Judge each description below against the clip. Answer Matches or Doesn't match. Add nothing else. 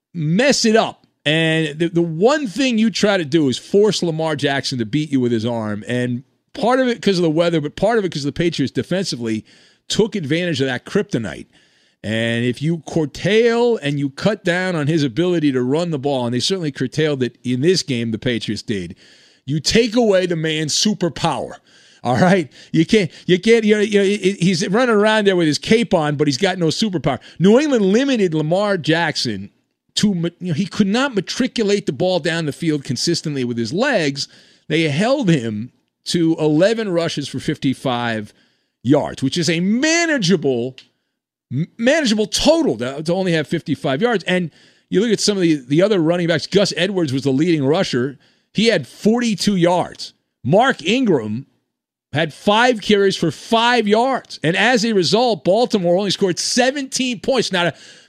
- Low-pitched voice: Doesn't match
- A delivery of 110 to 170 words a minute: Doesn't match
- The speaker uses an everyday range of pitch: Doesn't match